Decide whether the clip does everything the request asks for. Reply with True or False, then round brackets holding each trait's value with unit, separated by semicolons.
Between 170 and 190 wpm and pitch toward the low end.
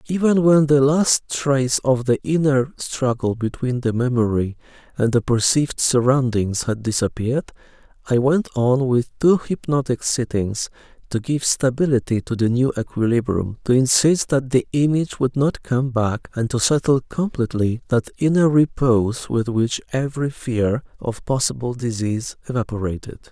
False (145 wpm; 130 Hz)